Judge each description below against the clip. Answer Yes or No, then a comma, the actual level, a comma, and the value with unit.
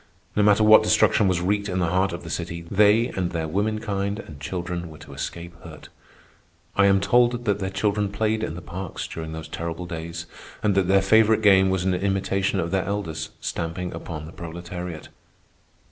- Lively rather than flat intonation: No, average, 3.3 semitones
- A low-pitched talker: Yes, very low, 95 Hz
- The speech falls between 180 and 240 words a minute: Yes, average, 190 wpm